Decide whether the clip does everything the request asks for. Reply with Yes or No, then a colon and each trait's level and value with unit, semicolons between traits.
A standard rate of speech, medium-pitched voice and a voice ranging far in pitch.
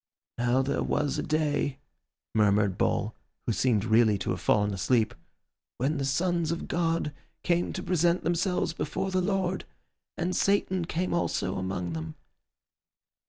Yes: average, 145 wpm; medium, 150 Hz; wide, 8.1 semitones